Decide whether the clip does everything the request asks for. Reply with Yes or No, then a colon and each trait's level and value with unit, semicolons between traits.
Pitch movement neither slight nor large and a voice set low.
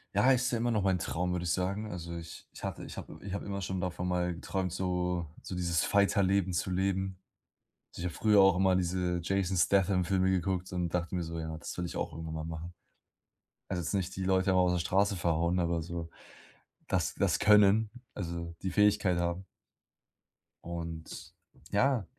No: narrow, 2.2 semitones; very low, 90 Hz